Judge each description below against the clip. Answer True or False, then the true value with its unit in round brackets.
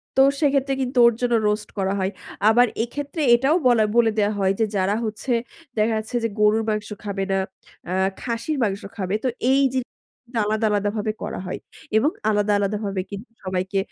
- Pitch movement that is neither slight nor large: True (3.2 semitones)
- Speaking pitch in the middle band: False (215 Hz)